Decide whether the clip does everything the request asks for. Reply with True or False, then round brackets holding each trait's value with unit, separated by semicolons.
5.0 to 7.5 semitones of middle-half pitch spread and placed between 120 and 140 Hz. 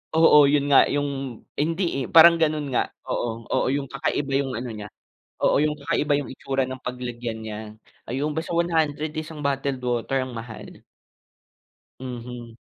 False (3.3 semitones; 135 Hz)